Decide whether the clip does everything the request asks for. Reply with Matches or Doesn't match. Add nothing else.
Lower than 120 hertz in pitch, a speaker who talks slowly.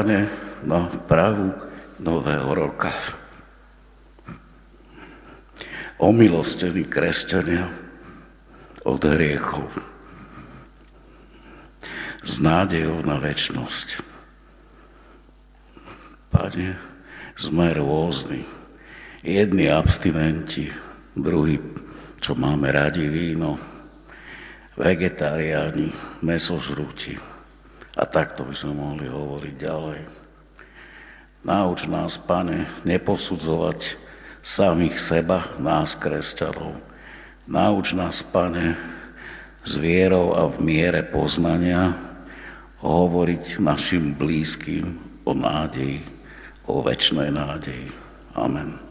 Matches